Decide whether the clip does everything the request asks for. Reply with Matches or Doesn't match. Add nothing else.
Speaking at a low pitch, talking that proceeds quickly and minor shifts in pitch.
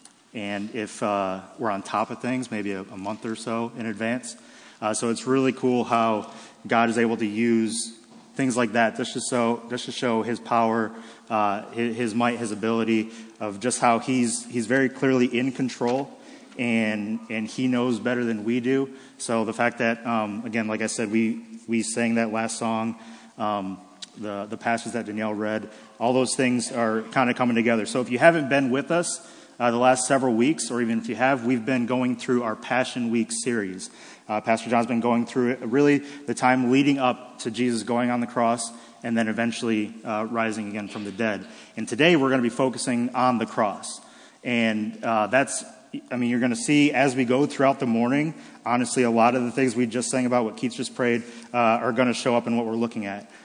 Matches